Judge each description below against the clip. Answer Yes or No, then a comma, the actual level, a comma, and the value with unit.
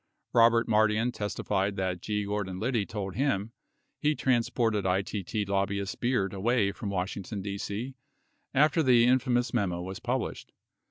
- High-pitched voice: No, low, 105 Hz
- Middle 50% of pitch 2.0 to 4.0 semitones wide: Yes, average, 3.6 semitones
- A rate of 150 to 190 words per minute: No, average, 140 wpm